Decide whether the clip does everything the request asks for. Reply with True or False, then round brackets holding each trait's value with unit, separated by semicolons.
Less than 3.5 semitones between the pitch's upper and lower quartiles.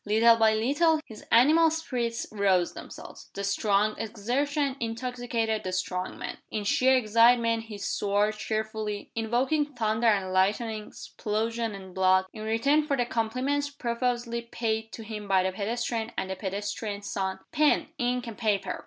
True (2.9 semitones)